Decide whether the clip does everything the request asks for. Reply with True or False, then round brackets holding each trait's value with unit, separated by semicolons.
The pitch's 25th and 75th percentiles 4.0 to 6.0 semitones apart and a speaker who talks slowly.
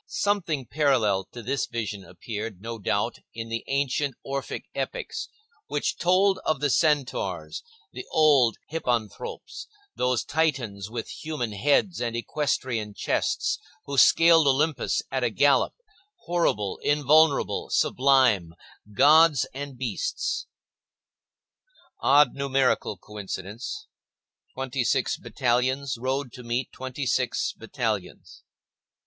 True (4.3 semitones; 105 wpm)